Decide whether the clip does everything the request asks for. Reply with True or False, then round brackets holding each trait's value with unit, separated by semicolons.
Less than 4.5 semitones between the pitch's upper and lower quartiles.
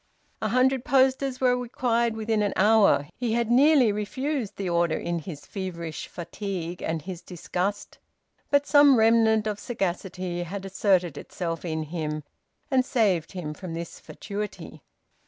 False (5.5 semitones)